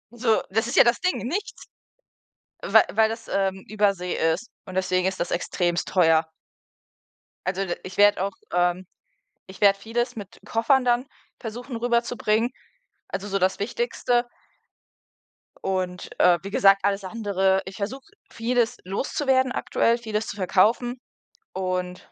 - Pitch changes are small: No, average, 4.0 semitones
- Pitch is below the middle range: No, high, 205 Hz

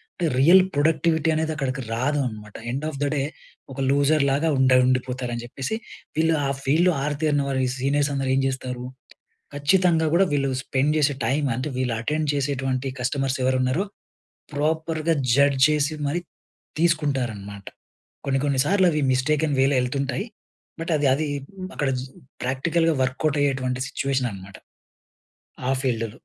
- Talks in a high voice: No, medium, 140 Hz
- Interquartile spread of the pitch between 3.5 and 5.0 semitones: No, average, 3.0 semitones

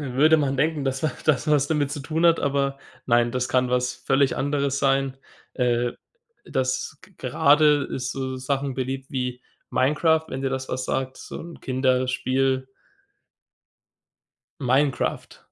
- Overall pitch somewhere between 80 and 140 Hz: Yes, low, 135 Hz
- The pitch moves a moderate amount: No, narrow, 1.8 semitones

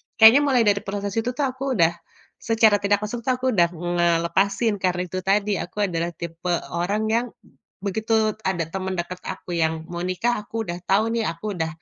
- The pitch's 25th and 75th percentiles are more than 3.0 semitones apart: Yes, average, 4.2 semitones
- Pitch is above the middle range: Yes, high, 195 Hz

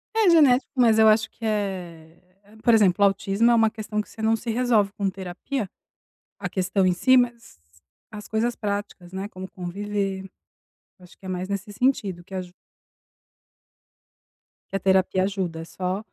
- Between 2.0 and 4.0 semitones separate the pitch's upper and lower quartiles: Yes, average, 2.9 semitones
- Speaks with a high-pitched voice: Yes, high, 200 Hz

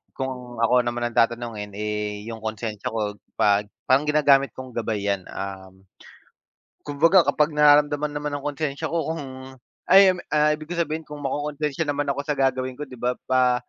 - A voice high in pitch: No, low, 130 Hz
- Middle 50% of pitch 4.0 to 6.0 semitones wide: Yes, average, 4.6 semitones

